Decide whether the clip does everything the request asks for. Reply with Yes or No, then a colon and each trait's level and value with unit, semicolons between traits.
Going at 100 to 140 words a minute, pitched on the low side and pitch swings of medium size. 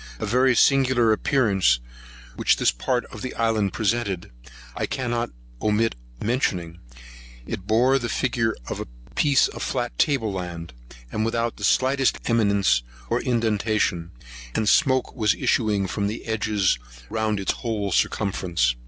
Yes: slow, 135 wpm; low, 110 Hz; average, 3.4 semitones